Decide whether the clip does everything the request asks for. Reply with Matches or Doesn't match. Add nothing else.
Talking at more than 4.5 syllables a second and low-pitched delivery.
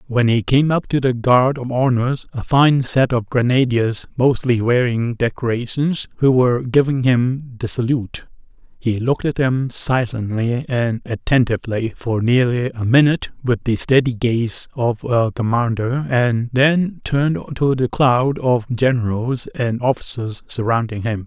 Doesn't match